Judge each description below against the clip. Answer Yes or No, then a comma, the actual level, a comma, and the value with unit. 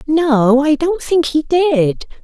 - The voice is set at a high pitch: Yes, very high, 295 Hz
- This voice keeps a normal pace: Yes, average, 160 wpm